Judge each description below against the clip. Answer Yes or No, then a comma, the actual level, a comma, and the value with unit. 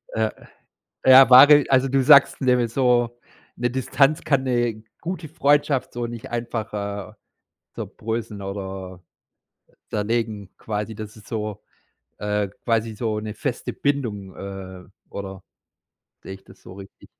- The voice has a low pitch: Yes, low, 115 Hz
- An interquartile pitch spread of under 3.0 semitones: No, average, 4.0 semitones